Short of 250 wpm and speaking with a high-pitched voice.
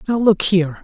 Yes: fast, 215 wpm; high, 195 Hz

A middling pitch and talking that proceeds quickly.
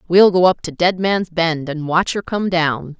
Yes: medium, 170 Hz; fast, 240 wpm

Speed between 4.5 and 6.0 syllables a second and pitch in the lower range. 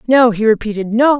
No: 5.6 syllables/s; high, 230 Hz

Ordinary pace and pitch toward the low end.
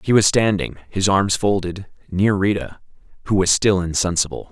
Yes: average, 160 wpm; very low, 95 Hz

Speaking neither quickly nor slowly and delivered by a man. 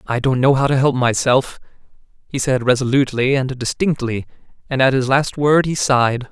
Yes: average, 180 wpm; male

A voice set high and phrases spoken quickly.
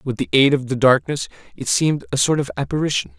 No: low, 135 Hz; fast, 225 wpm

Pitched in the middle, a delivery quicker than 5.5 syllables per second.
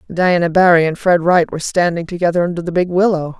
Yes: medium, 175 Hz; 6.3 syllables/s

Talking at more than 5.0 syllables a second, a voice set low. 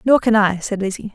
No: 5.7 syllables/s; high, 205 Hz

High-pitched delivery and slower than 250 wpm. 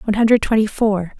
Yes: high, 210 Hz; average, 200 wpm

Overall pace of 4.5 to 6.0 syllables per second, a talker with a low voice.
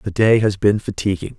Yes: 5.5 syllables/s; low, 100 Hz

